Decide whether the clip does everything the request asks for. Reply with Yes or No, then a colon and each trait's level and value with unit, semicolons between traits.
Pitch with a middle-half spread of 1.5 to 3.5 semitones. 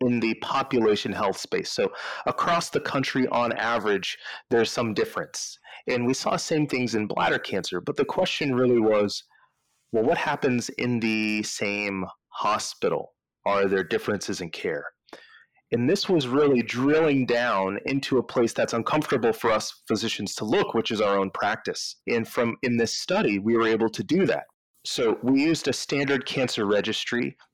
No: average, 4.3 semitones